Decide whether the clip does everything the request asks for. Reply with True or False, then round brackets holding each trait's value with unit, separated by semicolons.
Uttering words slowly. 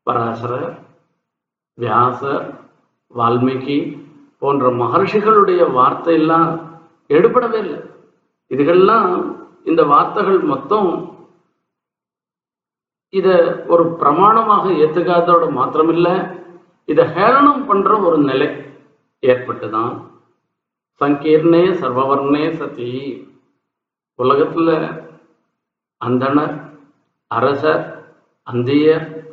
True (65 wpm)